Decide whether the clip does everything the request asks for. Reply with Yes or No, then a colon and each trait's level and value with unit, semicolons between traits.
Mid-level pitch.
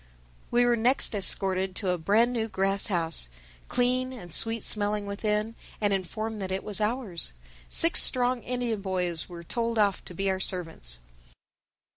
No: high, 205 Hz